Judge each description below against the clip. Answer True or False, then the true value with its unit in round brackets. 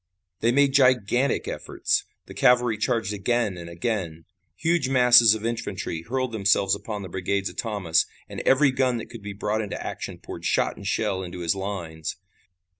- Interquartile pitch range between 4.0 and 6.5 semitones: True (4.3 semitones)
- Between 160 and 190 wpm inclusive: True (175 wpm)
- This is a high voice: False (110 Hz)